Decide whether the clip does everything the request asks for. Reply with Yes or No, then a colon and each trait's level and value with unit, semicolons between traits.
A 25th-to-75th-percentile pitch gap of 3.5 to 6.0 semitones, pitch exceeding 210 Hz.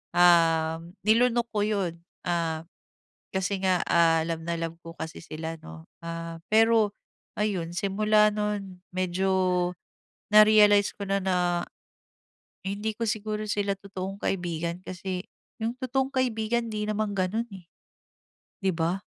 No: average, 3.8 semitones; high, 190 Hz